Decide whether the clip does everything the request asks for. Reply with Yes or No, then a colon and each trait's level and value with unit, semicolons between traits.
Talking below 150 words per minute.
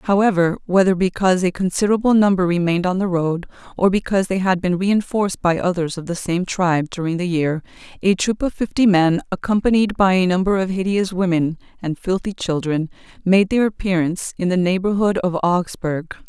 No: average, 175 wpm